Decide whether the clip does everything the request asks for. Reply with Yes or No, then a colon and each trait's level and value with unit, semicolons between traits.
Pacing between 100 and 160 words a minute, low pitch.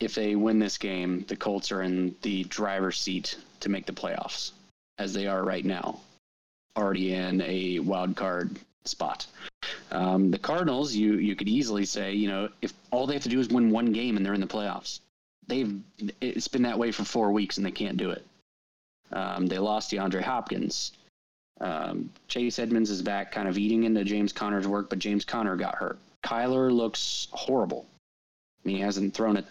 No: average, 195 wpm; low, 100 Hz